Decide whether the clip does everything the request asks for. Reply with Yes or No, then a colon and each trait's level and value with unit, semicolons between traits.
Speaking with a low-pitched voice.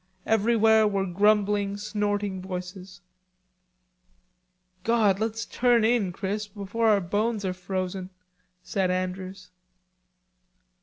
No: high, 200 Hz